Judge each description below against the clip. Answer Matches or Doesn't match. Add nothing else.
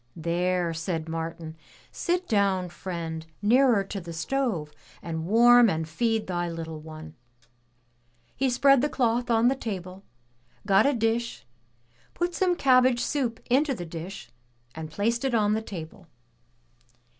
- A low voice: Doesn't match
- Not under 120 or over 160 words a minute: Matches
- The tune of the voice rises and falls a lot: Matches